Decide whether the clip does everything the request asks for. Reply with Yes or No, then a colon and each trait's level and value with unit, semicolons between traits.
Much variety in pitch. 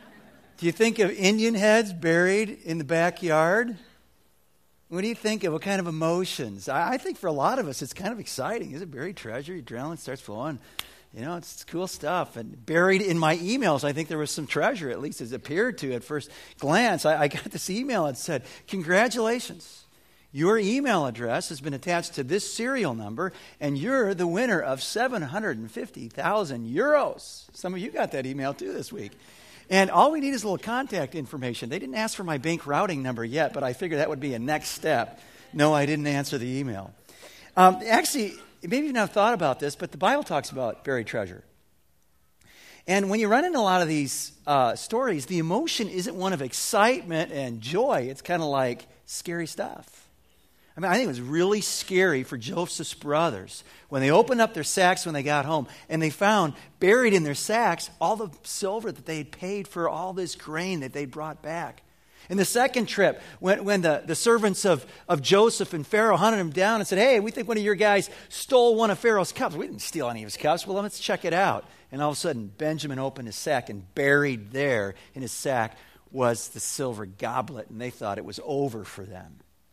Yes: wide, 6.7 semitones